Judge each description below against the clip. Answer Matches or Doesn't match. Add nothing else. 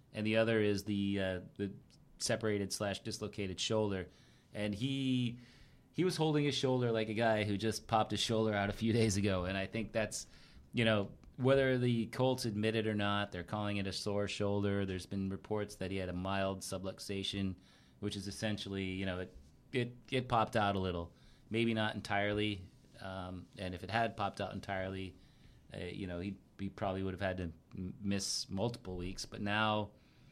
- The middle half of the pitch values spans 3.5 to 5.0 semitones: Doesn't match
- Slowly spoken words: Doesn't match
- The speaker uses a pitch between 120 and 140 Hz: Doesn't match